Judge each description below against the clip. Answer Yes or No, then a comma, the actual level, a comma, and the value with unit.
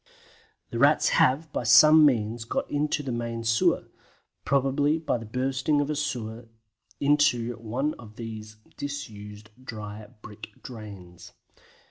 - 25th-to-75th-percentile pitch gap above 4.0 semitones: Yes, average, 4.9 semitones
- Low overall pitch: Yes, low, 120 Hz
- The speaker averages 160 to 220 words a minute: No, slow, 135 wpm